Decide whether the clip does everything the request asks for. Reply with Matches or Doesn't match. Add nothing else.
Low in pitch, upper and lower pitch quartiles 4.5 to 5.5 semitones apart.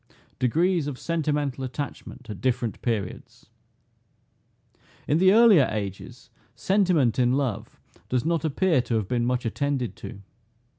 Matches